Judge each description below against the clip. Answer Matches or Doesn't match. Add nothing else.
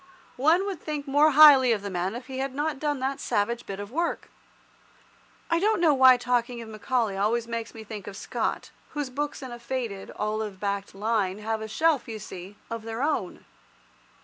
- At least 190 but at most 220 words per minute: Matches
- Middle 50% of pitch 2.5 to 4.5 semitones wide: Doesn't match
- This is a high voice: Matches